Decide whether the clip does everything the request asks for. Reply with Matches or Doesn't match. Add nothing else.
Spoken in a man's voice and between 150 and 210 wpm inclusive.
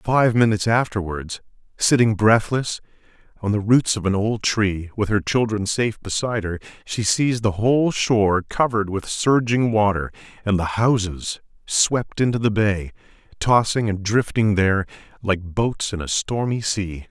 Matches